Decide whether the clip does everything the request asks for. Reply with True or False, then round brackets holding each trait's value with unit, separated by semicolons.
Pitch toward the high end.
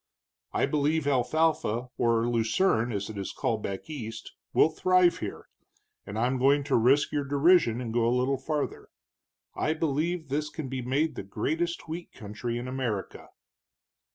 False (135 Hz)